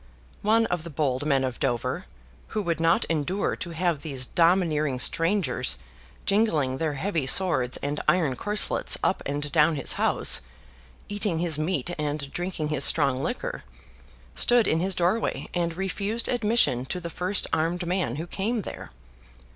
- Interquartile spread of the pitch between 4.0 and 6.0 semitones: Yes, average, 4.6 semitones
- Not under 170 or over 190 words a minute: No, average, 155 wpm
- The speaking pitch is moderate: Yes, medium, 165 Hz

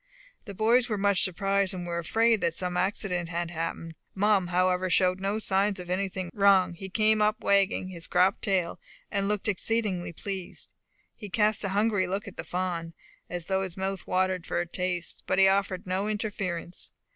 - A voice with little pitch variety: Yes, narrow, 2.0 semitones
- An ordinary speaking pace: Yes, average, 180 wpm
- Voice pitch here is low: No, high, 190 Hz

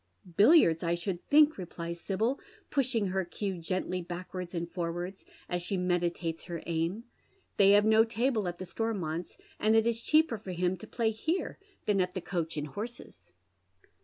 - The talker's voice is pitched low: No, medium, 185 Hz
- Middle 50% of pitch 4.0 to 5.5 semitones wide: Yes, average, 4.3 semitones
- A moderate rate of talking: Yes, average, 185 wpm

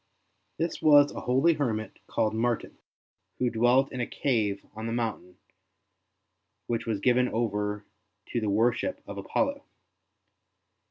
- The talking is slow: Yes, slow, 130 wpm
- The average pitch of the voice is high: No, low, 120 Hz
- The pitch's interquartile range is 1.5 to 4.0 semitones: Yes, average, 3.4 semitones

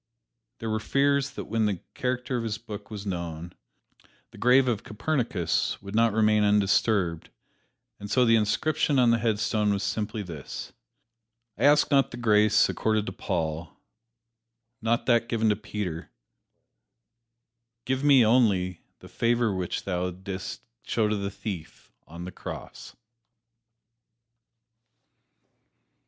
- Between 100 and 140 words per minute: Yes, slow, 135 wpm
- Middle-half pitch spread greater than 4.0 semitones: No, average, 3.2 semitones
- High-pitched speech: No, low, 105 Hz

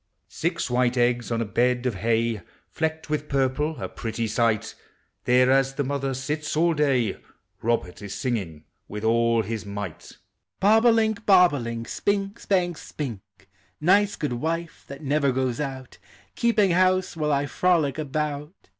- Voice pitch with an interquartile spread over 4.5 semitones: Yes, wide, 5.4 semitones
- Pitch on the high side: No, low, 135 Hz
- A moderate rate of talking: Yes, average, 160 wpm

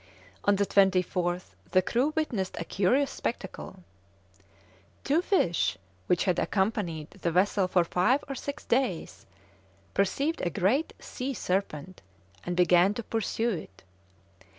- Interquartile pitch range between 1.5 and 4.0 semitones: No, average, 5.1 semitones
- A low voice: No, high, 190 Hz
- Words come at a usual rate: No, slow, 130 wpm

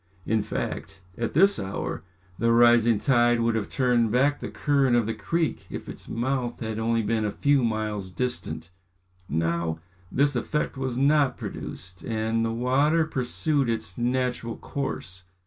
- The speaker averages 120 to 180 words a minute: Yes, average, 155 wpm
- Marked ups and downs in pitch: No, average, 3.3 semitones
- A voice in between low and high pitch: No, low, 120 Hz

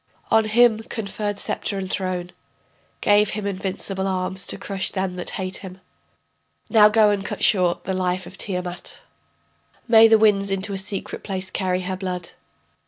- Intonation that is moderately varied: No, narrow, 2.1 semitones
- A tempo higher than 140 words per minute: Yes, average, 165 wpm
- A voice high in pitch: Yes, high, 195 Hz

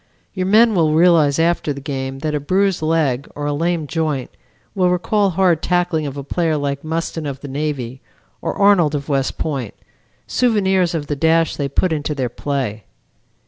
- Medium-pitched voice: Yes, medium, 155 Hz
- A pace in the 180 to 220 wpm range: Yes, average, 185 wpm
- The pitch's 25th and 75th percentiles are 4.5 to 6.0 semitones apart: No, average, 3.8 semitones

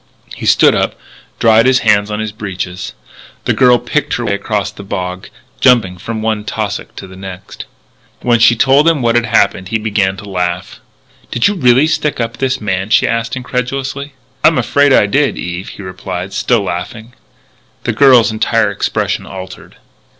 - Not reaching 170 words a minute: No, average, 175 wpm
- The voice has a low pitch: Yes, low, 110 Hz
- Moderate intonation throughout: Yes, average, 4.5 semitones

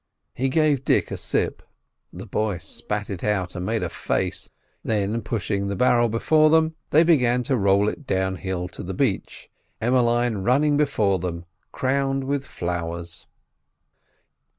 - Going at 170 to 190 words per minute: No, average, 150 wpm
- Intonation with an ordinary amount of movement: No, wide, 6.0 semitones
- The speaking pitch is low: Yes, low, 110 Hz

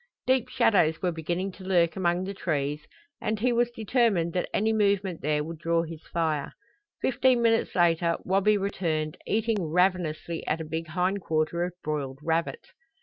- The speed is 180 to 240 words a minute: No, average, 165 wpm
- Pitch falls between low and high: Yes, medium, 175 Hz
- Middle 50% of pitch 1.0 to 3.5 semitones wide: No, average, 3.9 semitones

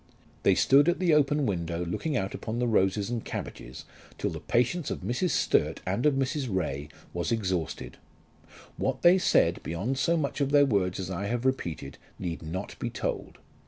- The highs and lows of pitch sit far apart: Yes, wide, 7.4 semitones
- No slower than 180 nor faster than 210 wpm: Yes, average, 185 wpm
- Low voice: Yes, low, 115 Hz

